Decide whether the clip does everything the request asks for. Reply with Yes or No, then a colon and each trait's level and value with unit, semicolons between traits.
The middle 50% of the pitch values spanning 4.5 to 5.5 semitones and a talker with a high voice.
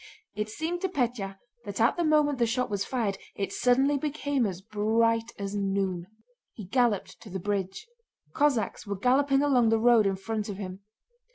Yes: average, 4.9 semitones; high, 225 Hz